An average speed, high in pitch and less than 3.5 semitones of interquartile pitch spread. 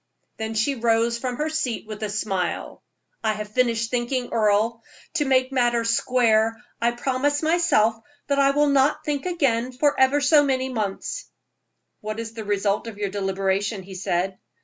No: average, 170 wpm; high, 235 Hz; average, 3.9 semitones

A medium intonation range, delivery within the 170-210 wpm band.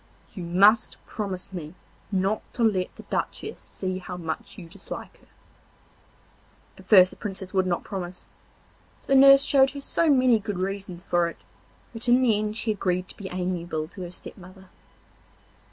Yes: average, 3.2 semitones; average, 175 wpm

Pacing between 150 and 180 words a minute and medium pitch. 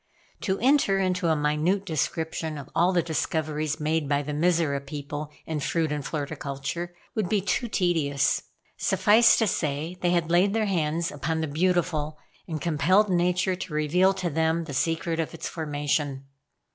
Yes: average, 165 wpm; medium, 160 Hz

